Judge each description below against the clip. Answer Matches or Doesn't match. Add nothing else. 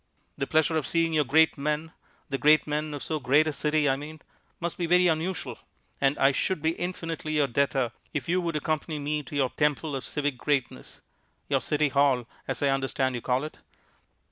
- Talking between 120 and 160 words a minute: Doesn't match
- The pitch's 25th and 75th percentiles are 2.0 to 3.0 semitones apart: Matches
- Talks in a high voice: Doesn't match